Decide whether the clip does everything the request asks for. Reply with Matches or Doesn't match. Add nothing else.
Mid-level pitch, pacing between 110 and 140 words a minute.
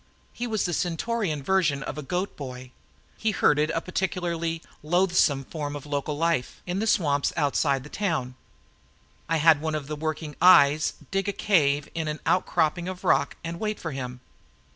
Doesn't match